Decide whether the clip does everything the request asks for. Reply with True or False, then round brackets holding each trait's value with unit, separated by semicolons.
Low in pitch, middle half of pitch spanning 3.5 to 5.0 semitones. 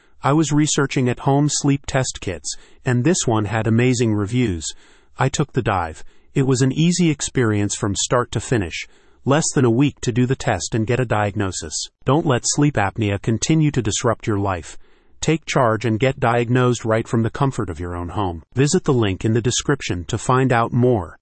True (120 Hz; 4.5 semitones)